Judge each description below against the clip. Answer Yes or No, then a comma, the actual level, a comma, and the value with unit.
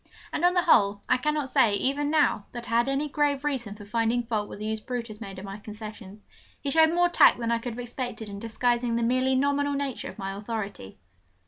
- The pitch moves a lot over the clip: No, average, 4.7 semitones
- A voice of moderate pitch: No, high, 235 Hz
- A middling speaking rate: No, fast, 230 wpm